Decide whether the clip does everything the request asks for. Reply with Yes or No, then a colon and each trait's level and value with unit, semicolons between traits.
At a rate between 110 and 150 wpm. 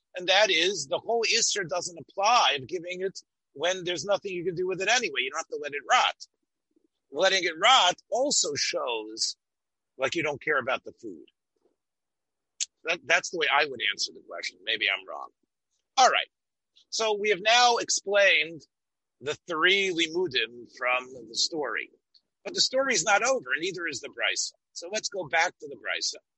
No: average, 185 wpm